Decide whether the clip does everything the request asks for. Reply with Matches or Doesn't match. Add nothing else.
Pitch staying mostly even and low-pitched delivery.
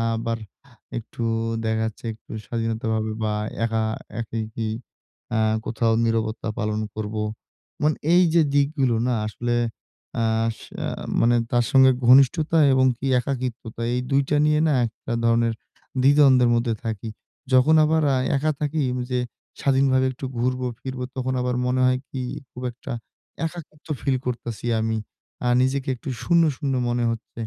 Doesn't match